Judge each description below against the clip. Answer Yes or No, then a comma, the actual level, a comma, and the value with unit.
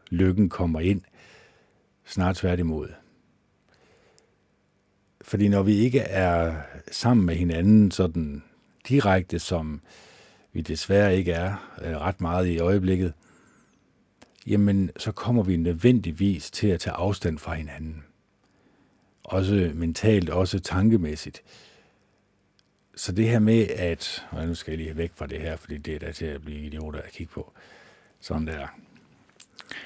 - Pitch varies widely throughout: No, average, 3.8 semitones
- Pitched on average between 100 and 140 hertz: No, very low, 90 Hz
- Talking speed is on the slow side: Yes, slow, 135 wpm